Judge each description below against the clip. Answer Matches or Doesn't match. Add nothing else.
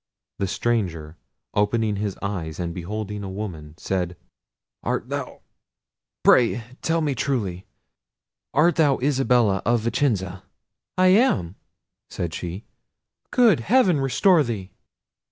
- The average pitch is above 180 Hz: Doesn't match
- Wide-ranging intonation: Matches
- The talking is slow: Matches